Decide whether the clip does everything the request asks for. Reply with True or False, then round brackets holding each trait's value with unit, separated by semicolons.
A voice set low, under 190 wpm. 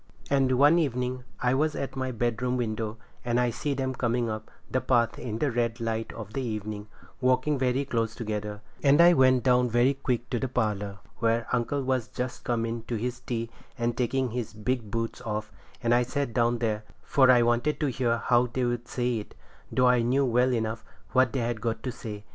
False (120 Hz; 205 wpm)